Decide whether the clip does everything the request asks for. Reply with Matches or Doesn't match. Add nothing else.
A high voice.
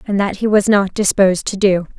Matches